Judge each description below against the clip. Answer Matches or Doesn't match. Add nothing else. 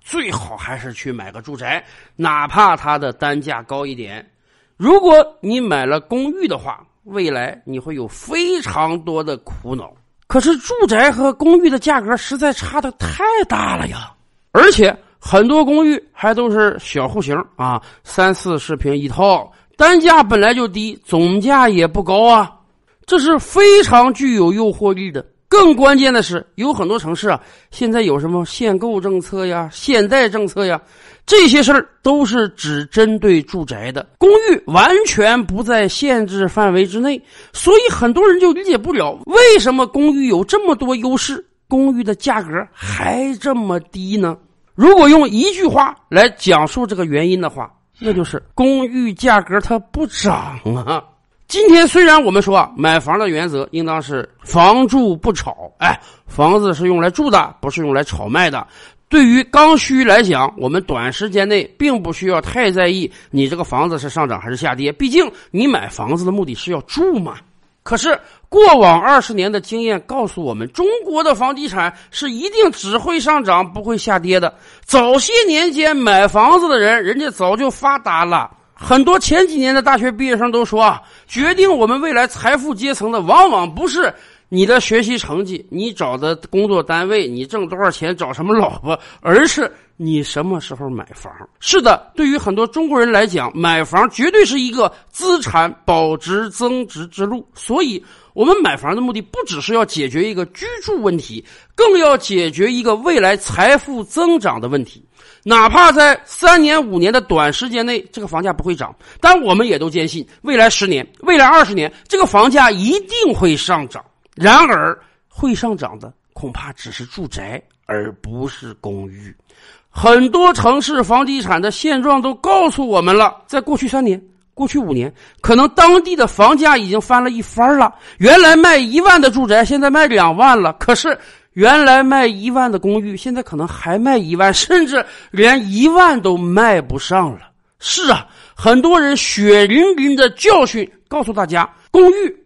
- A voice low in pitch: Doesn't match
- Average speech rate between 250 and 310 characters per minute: Matches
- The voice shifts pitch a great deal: Matches